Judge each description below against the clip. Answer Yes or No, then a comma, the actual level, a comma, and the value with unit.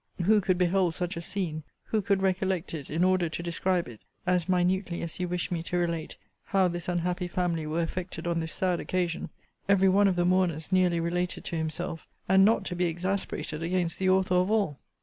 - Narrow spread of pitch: Yes, narrow, 1.8 semitones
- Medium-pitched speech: Yes, medium, 180 Hz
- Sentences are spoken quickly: Yes, fast, 210 wpm